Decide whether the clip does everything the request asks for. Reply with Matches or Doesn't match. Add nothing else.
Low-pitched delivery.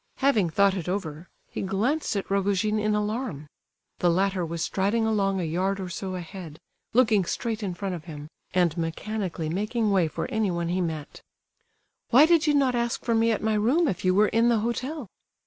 Doesn't match